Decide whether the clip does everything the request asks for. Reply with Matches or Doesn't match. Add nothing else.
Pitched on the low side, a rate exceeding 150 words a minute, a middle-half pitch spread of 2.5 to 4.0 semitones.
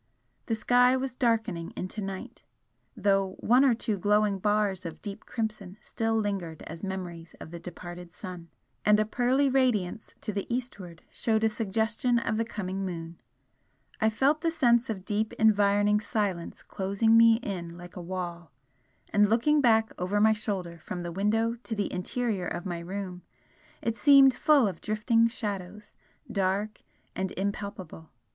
Doesn't match